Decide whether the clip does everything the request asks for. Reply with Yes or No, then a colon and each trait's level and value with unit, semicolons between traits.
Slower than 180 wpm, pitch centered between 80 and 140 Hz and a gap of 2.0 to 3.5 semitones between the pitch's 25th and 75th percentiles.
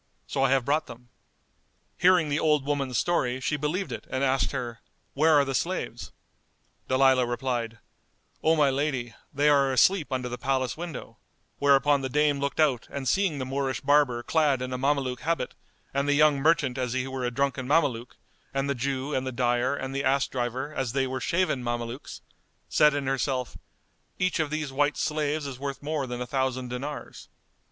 No: average, 190 wpm; low, 135 Hz; narrow, 2.4 semitones